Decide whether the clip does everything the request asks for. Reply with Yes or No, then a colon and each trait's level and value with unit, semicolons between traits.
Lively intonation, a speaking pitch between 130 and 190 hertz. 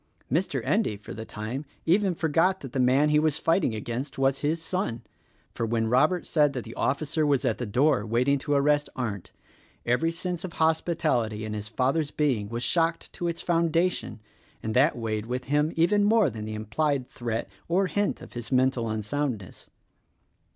Yes: wide, 6.0 semitones; medium, 140 Hz